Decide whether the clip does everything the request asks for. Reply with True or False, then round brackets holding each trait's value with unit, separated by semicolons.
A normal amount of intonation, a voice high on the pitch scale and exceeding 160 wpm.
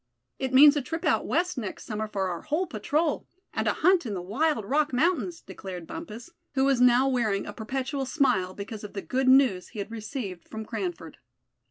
False (6.0 semitones; 255 Hz; 200 wpm)